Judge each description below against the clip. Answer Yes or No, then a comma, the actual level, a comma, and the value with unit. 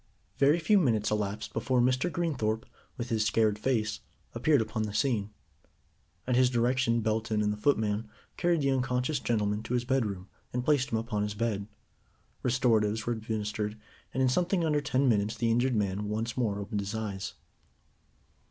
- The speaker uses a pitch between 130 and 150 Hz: No, low, 115 Hz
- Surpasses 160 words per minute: Yes, average, 170 wpm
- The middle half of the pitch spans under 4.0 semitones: Yes, average, 3.3 semitones